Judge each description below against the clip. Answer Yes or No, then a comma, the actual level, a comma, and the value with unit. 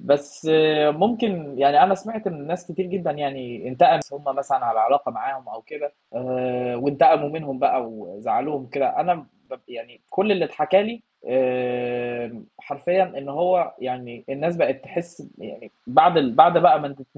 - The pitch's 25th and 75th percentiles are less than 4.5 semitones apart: No, wide, 5.5 semitones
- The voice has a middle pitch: Yes, medium, 145 Hz